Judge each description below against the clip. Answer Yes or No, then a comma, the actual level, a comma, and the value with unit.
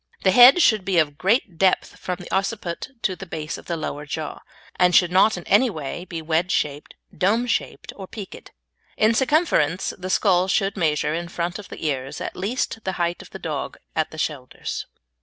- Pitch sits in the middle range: Yes, medium, 180 Hz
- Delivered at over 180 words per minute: Yes, average, 200 wpm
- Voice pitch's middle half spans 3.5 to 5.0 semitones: Yes, average, 3.8 semitones